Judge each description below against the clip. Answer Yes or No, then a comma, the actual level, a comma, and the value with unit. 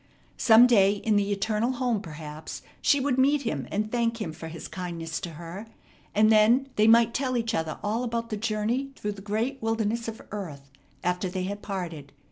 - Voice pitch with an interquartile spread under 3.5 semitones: No, average, 4.2 semitones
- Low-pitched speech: No, high, 215 Hz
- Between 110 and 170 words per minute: No, average, 195 wpm